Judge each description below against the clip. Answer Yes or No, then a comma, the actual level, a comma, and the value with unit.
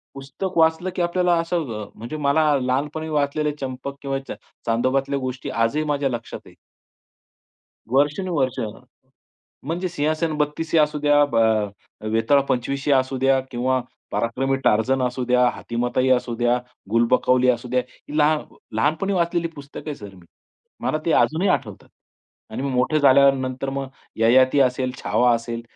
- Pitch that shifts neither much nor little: Yes, average, 3.3 semitones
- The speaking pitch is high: No, low, 135 Hz